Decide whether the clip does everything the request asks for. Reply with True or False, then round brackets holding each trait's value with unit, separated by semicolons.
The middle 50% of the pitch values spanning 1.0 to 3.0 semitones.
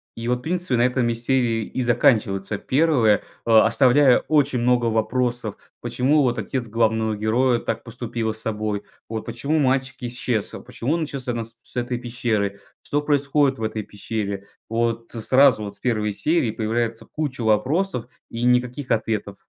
True (2.7 semitones)